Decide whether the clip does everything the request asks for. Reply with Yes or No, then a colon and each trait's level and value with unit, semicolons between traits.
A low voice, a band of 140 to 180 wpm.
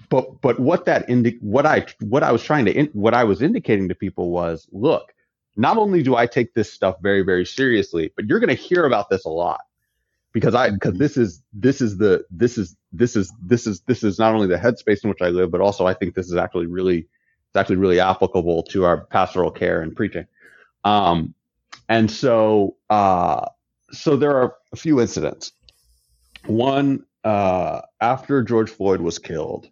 No: low, 105 Hz; fast, 205 wpm